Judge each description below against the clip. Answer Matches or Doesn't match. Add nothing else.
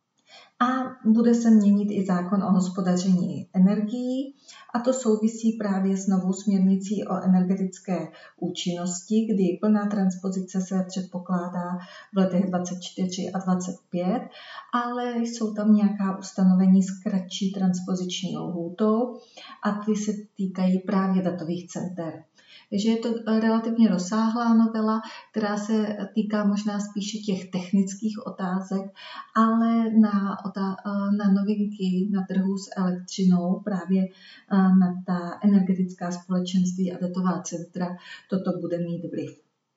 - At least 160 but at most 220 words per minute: Doesn't match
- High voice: Matches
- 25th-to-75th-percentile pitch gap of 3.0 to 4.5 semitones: Doesn't match